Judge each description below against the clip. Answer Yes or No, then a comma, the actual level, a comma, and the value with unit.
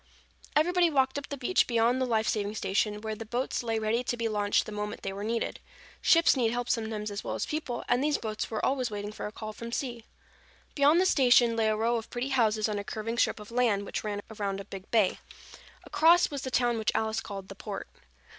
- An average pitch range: Yes, average, 3.0 semitones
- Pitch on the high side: Yes, high, 225 Hz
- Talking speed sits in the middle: No, fast, 235 wpm